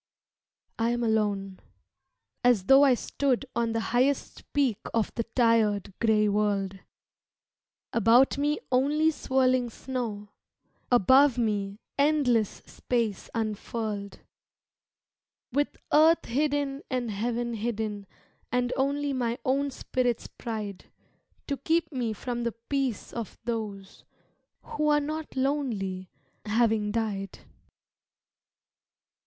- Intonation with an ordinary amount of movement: Yes, average, 4.1 semitones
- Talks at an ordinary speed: No, slow, 105 wpm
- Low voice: No, high, 235 Hz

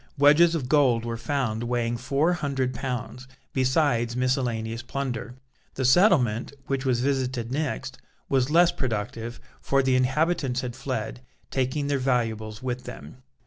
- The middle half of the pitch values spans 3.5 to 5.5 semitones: No, narrow, 2.6 semitones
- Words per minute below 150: Yes, average, 140 wpm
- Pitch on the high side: No, low, 130 Hz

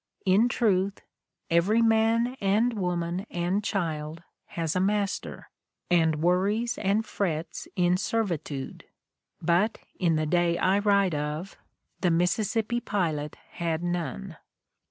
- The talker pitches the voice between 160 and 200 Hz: Yes, medium, 185 Hz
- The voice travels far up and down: No, average, 3.7 semitones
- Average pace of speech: No, slow, 115 wpm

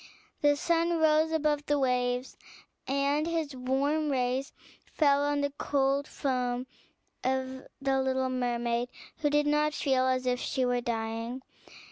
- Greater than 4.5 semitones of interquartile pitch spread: No, average, 2.7 semitones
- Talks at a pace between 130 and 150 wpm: Yes, average, 140 wpm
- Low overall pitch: No, very high, 270 Hz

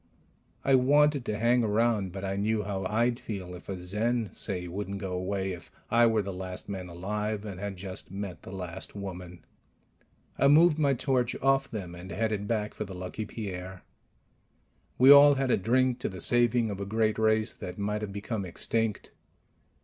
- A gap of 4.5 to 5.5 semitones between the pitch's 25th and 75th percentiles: No, average, 3.8 semitones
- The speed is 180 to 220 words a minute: Yes, average, 190 wpm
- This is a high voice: No, low, 105 Hz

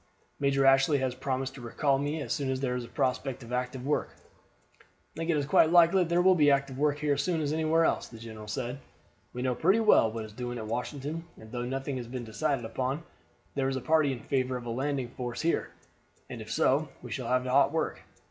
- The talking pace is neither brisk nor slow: No, fast, 245 wpm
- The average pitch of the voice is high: No, low, 135 Hz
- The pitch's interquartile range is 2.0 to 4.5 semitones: Yes, average, 3.1 semitones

